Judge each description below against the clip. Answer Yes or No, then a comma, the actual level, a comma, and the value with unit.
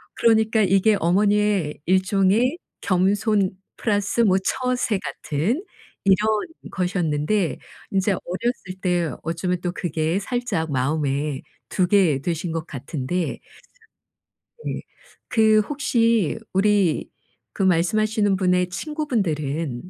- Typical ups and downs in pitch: Yes, average, 4.4 semitones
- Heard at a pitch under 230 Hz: Yes, high, 190 Hz